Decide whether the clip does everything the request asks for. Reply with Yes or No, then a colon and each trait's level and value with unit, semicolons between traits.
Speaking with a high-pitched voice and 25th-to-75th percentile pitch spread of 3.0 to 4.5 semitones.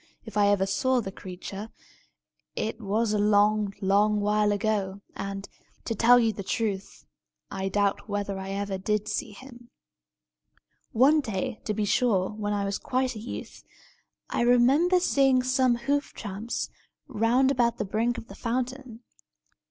Yes: high, 215 Hz; average, 3.4 semitones